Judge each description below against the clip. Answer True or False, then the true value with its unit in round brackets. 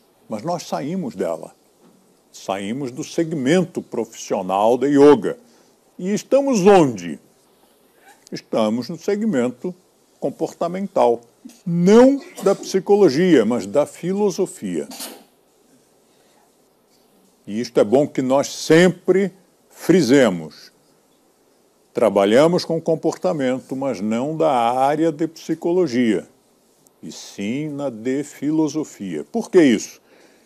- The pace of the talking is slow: True (95 wpm)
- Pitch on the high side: False (170 Hz)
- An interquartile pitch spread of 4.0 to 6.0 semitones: True (5.1 semitones)